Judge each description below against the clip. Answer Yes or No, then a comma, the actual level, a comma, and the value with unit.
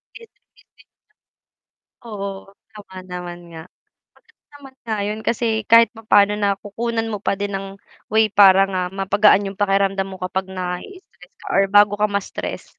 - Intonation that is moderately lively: No, narrow, 2.2 semitones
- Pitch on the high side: Yes, high, 200 Hz